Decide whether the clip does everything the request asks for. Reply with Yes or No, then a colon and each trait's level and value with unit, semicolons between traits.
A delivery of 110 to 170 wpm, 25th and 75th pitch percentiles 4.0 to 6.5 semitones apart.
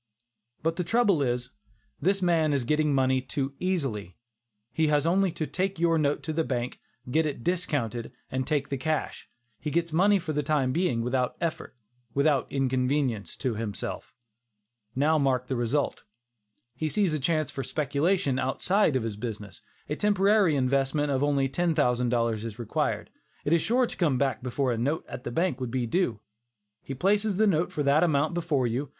No: average, 180 wpm; average, 4.6 semitones